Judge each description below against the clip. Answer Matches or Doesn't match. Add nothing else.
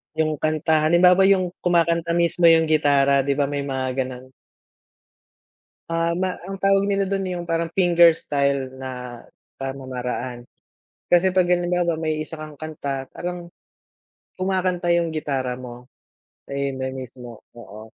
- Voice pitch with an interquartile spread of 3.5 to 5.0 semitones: Matches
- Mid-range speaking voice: Matches